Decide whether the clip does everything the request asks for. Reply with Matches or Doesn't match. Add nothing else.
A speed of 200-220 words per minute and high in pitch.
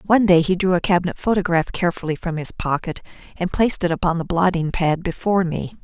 Doesn't match